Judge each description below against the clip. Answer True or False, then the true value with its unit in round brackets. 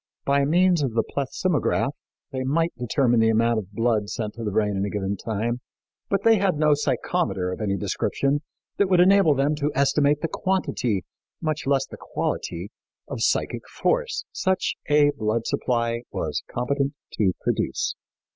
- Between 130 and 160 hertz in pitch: True (135 Hz)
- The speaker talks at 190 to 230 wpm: False (165 wpm)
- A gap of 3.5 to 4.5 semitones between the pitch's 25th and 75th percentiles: False (5.5 semitones)